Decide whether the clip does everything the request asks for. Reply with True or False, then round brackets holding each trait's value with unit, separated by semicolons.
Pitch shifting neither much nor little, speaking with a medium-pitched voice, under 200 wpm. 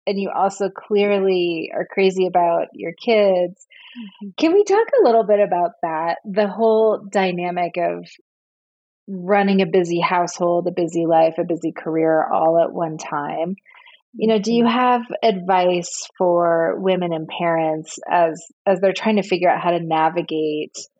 True (3.4 semitones; 180 Hz; 155 wpm)